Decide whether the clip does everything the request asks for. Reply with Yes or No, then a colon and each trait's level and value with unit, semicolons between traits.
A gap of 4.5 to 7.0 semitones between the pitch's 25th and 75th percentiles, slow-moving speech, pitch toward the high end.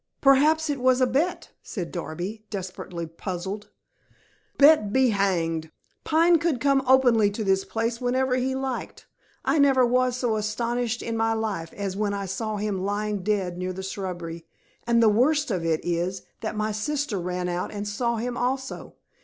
No: average, 5.1 semitones; average, 170 wpm; high, 215 Hz